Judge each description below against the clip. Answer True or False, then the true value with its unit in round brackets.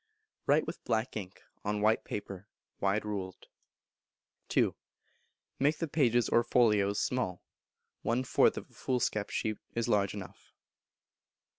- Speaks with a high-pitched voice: False (110 Hz)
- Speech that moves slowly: True (130 wpm)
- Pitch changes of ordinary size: True (3.2 semitones)